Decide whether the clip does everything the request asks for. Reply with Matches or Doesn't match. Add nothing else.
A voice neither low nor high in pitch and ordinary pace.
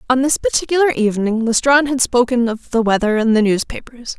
Doesn't match